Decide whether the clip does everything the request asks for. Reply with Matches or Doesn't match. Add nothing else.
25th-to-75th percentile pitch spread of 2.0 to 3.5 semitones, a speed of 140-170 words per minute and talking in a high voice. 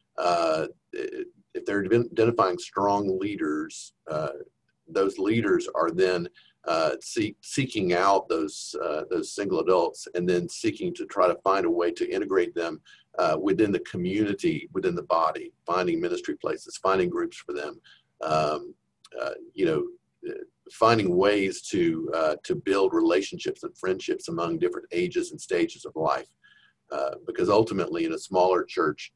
Matches